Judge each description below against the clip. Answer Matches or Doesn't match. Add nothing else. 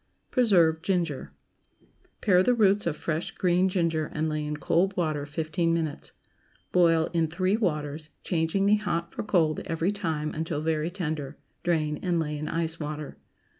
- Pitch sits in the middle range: Matches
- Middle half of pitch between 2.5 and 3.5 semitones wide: Matches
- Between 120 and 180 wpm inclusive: Matches